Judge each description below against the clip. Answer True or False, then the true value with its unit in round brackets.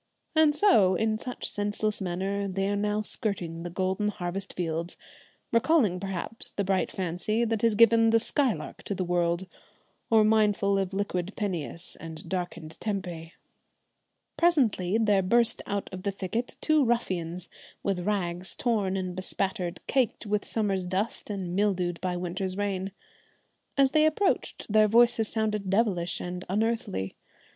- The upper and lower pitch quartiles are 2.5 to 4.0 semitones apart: True (3.4 semitones)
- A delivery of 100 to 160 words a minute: True (145 wpm)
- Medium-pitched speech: False (200 Hz)